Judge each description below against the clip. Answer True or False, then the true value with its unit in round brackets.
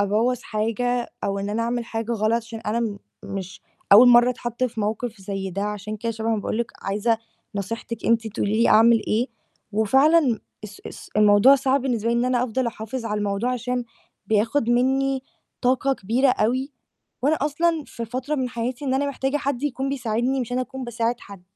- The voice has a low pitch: False (235 Hz)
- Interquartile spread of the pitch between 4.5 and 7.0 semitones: False (3.0 semitones)